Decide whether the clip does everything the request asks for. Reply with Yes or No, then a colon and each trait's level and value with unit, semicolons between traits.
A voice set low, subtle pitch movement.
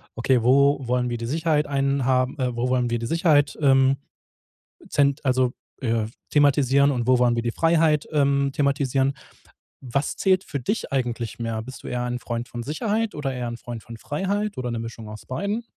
No: low, 130 Hz; average, 3.2 semitones